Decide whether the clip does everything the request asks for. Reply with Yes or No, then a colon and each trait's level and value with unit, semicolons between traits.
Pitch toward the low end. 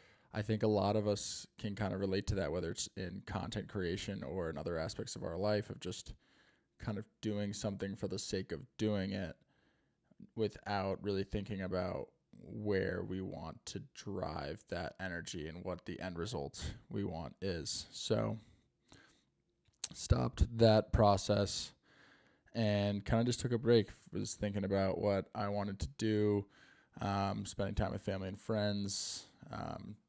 Yes: low, 100 Hz